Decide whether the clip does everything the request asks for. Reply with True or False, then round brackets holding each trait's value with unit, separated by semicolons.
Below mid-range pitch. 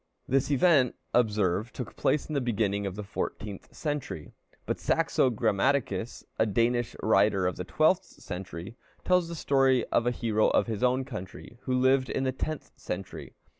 True (120 Hz)